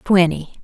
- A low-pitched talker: No, medium, 175 Hz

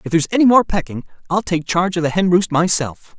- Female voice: No, male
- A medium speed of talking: No, fast, 245 wpm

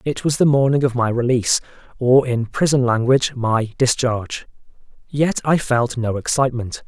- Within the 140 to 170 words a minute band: Yes, average, 155 wpm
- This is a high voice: No, low, 125 Hz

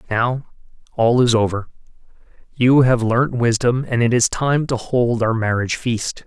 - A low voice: Yes, low, 120 Hz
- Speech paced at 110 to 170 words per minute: Yes, average, 165 wpm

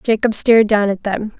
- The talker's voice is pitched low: No, high, 210 Hz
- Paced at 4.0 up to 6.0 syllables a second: Yes, 5.3 syllables/s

